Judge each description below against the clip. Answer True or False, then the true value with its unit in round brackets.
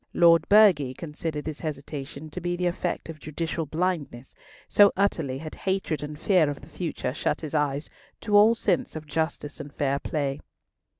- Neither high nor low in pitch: True (155 Hz)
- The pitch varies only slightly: False (3.4 semitones)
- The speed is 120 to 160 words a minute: False (170 wpm)